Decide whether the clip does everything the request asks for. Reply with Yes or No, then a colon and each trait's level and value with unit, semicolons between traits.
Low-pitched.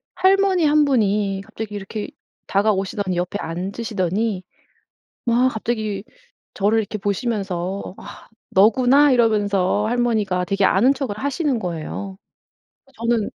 No: high, 210 Hz